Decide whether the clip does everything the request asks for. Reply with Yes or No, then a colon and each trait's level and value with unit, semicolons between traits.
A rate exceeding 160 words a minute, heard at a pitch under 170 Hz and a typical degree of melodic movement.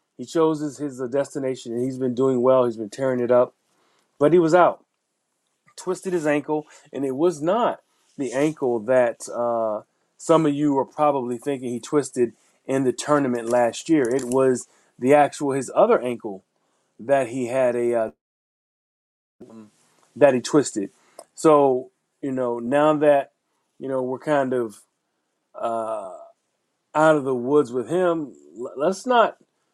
No: average, 155 wpm; low, 135 Hz; average, 3.3 semitones